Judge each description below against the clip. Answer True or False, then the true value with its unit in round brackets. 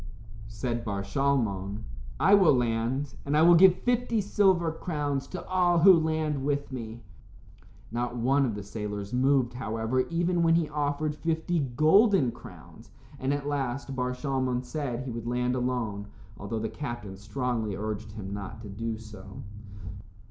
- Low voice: True (130 Hz)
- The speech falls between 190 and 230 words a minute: False (155 wpm)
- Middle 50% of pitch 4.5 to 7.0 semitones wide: True (5.4 semitones)